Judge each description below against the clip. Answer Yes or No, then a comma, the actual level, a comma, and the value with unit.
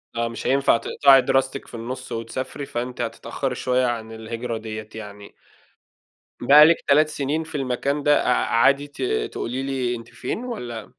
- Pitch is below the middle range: Yes, low, 125 Hz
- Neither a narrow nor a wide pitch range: Yes, average, 3.2 semitones